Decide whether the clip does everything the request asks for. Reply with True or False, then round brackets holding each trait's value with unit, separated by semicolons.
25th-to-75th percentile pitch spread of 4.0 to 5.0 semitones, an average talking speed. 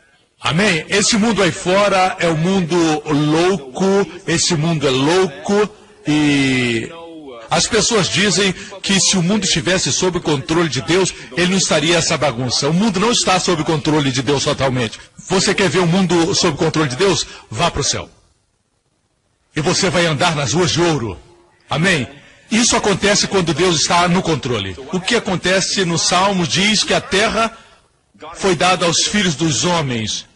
True (4.4 semitones; 175 wpm)